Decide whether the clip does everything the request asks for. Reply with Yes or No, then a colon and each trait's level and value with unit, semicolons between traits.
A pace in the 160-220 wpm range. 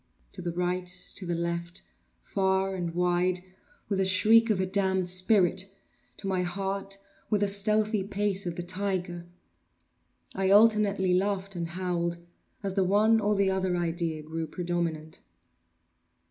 No: slow, 135 wpm